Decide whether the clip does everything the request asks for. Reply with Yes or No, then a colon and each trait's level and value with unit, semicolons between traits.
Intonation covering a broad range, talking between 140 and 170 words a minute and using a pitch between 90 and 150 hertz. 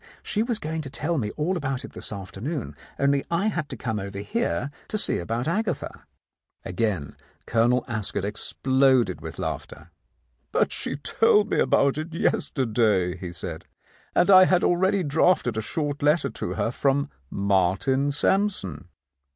Yes: wide, 8.0 semitones; average, 155 wpm; low, 135 Hz